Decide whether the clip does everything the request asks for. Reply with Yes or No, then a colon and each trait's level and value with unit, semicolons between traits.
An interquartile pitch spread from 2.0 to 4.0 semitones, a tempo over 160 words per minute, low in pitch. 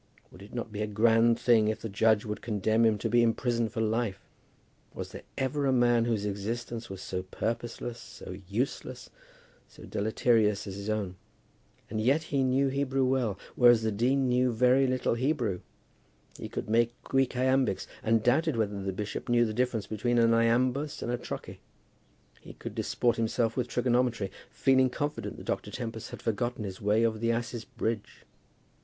Yes: narrow, 2.5 semitones; average, 180 wpm; low, 115 Hz